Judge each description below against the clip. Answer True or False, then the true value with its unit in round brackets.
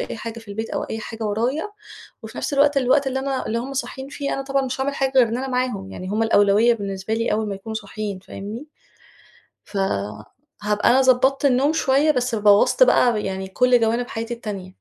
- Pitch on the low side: False (230 Hz)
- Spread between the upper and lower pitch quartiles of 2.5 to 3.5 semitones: False (4.2 semitones)